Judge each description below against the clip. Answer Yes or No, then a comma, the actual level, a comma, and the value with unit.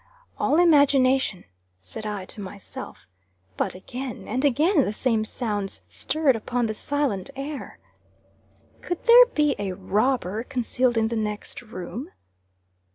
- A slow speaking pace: Yes, slow, 130 wpm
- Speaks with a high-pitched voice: Yes, high, 240 Hz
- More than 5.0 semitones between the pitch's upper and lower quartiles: Yes, wide, 5.4 semitones